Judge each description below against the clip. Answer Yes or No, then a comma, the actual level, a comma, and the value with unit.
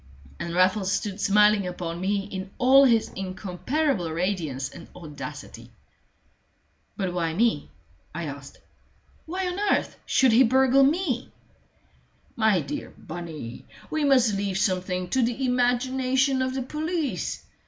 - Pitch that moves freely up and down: Yes, wide, 6.5 semitones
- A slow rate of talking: Yes, slow, 130 wpm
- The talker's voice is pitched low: No, high, 210 Hz